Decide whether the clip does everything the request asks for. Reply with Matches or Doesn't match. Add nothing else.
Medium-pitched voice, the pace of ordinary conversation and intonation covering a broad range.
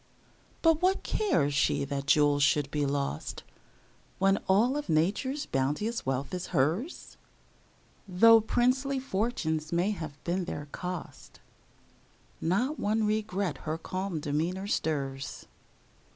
Doesn't match